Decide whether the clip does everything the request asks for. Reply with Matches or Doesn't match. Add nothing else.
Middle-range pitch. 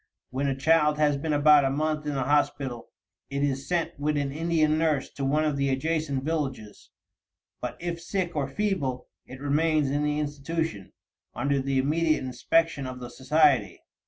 Matches